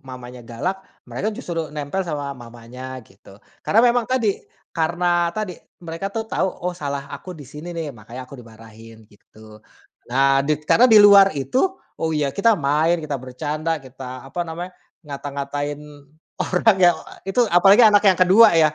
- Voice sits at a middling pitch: Yes, medium, 150 Hz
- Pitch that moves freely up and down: Yes, wide, 6.1 semitones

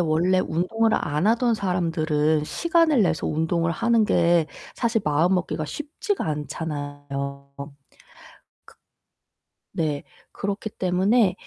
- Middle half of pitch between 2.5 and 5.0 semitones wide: No, wide, 5.5 semitones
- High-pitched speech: No, medium, 170 Hz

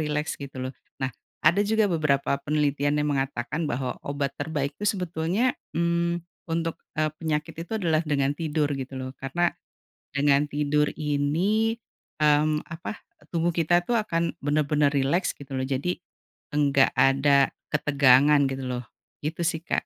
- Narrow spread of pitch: No, average, 3.1 semitones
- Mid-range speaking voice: Yes, medium, 150 Hz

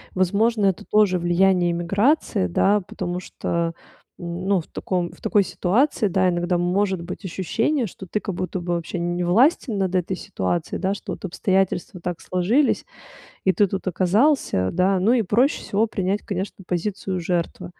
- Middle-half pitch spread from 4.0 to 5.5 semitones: No, average, 2.7 semitones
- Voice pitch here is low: No, medium, 185 Hz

